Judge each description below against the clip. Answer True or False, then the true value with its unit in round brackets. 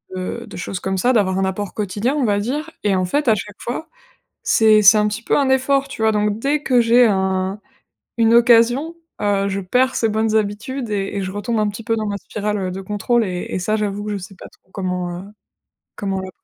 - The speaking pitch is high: True (210 Hz)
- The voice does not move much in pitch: False (3.3 semitones)